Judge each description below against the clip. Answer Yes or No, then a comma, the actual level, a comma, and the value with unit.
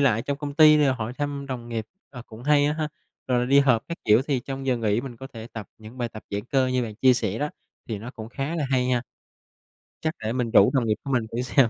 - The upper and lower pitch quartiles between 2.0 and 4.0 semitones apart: Yes, average, 3.5 semitones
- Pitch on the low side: Yes, low, 125 Hz